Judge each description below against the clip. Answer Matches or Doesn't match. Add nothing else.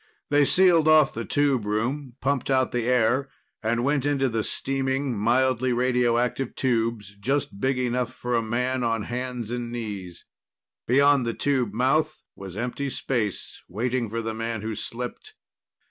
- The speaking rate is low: Doesn't match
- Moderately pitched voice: Doesn't match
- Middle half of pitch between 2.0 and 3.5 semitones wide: Matches